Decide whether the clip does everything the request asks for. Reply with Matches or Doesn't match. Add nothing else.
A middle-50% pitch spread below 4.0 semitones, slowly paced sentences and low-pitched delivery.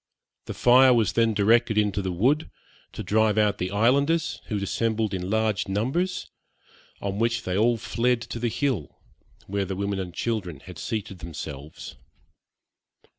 Doesn't match